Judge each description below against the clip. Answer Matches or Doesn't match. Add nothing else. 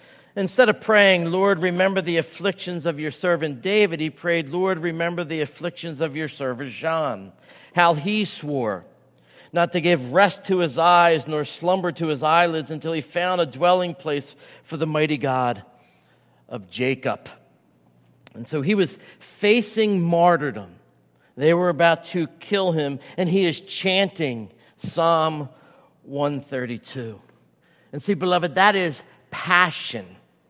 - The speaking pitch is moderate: Matches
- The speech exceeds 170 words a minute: Doesn't match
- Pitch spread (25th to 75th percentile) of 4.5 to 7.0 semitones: Doesn't match